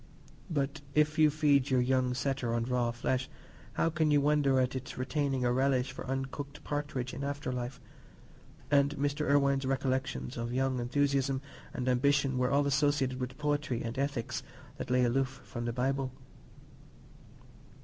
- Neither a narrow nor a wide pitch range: No, narrow, 2.1 semitones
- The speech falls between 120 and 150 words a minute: No, average, 160 wpm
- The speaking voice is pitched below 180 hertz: Yes, low, 135 Hz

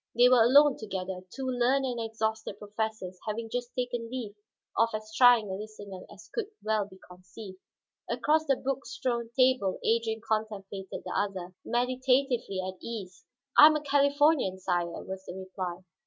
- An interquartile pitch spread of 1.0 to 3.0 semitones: No, average, 4.7 semitones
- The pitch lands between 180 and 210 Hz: No, high, 220 Hz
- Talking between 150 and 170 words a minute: Yes, average, 160 wpm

